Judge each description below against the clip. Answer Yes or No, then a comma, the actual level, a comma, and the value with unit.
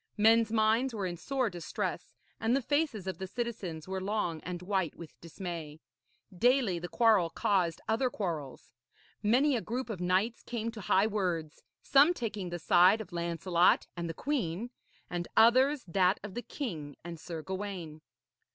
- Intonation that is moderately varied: Yes, average, 4.9 semitones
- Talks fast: No, average, 165 wpm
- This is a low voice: No, high, 195 Hz